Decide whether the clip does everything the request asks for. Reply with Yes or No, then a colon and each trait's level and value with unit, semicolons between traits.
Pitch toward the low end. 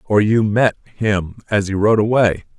Yes: low, 105 Hz